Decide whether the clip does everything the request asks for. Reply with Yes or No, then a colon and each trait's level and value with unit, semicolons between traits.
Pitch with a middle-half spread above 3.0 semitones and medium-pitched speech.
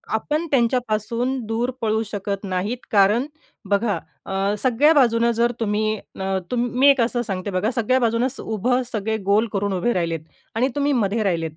No: average, 3.4 semitones; high, 225 Hz